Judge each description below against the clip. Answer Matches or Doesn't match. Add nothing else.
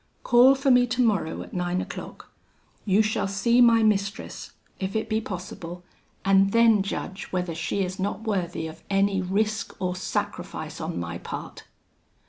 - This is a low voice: Doesn't match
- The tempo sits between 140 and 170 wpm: Matches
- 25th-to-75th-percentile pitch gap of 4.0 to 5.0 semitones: Doesn't match